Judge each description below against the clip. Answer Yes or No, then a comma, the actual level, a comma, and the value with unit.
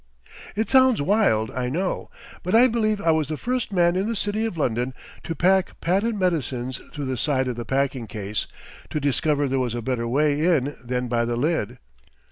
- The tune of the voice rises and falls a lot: Yes, wide, 7.3 semitones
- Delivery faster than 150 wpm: Yes, average, 200 wpm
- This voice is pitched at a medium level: Yes, medium, 145 Hz